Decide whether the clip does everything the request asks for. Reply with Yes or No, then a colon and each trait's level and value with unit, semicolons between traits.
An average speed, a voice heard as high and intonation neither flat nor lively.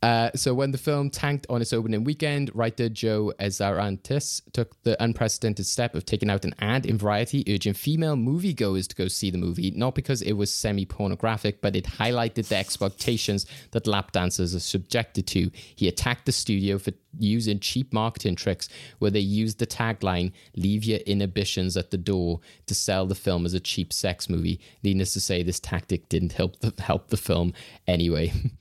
No: average, 190 wpm; low, 105 Hz; average, 3.6 semitones